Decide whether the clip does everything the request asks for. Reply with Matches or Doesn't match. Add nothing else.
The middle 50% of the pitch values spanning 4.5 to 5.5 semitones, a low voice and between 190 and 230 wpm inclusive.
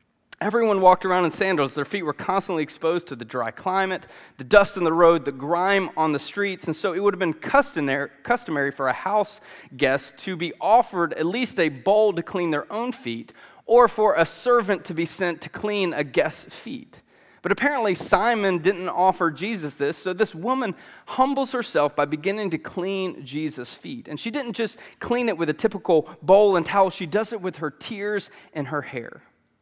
Doesn't match